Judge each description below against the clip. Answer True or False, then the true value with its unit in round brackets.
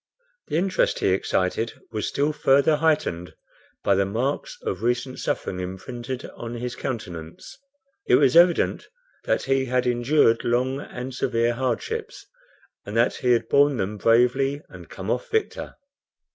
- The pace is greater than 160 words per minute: False (145 wpm)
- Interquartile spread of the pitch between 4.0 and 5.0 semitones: False (3.5 semitones)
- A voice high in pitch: False (125 Hz)